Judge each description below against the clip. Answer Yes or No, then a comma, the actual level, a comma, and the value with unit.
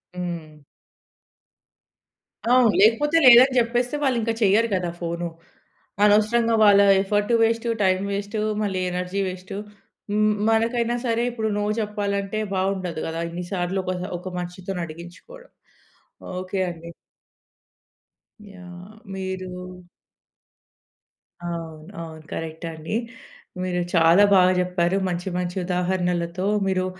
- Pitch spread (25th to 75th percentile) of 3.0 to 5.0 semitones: Yes, average, 3.5 semitones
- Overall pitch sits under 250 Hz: Yes, high, 190 Hz